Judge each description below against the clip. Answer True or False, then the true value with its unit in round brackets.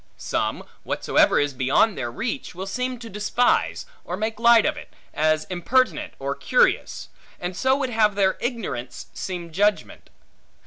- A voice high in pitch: True (210 Hz)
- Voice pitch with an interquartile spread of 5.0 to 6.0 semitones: True (5.4 semitones)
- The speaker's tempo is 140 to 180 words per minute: True (150 wpm)